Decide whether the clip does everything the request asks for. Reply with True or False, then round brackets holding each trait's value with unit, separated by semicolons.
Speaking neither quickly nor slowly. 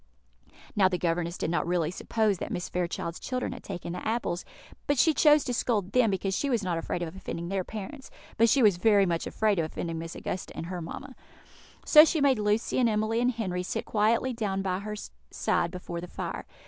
False (215 wpm)